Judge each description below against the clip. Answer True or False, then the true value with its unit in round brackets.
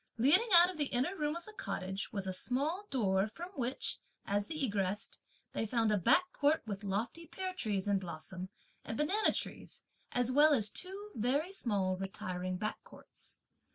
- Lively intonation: True (8.7 semitones)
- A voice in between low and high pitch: False (240 Hz)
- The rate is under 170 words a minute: False (180 wpm)